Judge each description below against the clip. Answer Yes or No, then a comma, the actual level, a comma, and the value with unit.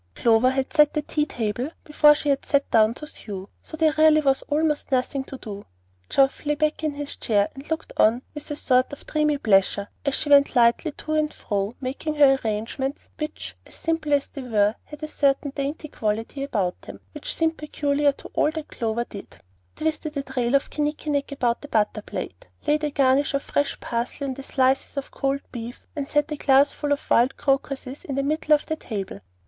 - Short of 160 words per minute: No, fast, 205 wpm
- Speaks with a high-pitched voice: Yes, very high, 280 Hz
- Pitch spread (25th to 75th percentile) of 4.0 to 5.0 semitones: No, average, 3.6 semitones